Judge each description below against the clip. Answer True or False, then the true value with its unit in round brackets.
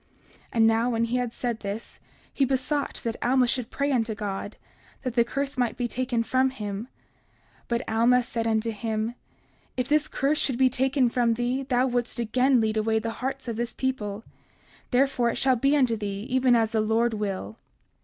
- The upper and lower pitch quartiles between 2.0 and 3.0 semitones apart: True (2.6 semitones)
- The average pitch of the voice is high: True (240 Hz)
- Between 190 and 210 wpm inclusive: True (195 wpm)